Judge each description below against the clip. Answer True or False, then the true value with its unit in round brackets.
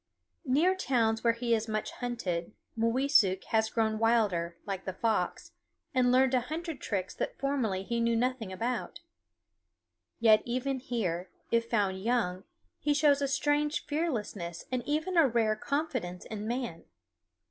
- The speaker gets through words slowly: False (145 wpm)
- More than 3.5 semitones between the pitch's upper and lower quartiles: True (4.0 semitones)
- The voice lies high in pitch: True (235 Hz)